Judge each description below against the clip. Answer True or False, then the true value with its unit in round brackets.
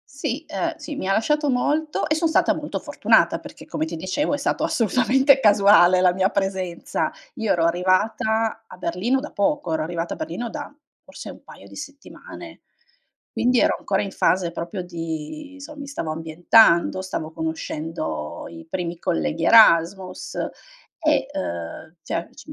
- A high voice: True (195 Hz)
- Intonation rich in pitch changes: True (8.6 semitones)